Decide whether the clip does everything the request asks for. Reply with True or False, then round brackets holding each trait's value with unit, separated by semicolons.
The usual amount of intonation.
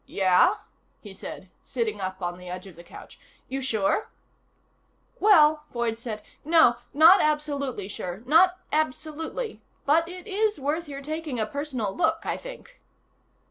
False (7.4 semitones)